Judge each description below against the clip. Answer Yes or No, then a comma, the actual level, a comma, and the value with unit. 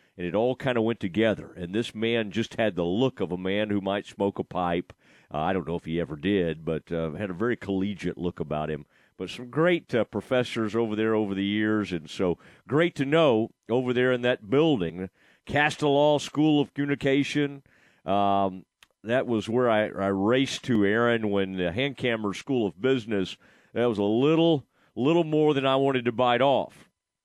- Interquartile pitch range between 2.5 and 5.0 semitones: No, wide, 5.4 semitones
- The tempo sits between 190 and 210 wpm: Yes, average, 200 wpm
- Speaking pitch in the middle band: No, low, 110 Hz